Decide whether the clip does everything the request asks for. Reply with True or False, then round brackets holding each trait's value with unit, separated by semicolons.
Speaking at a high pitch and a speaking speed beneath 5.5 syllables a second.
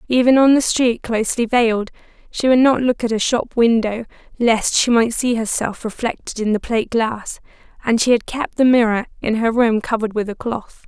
True (235 Hz; 5.3 syllables/s)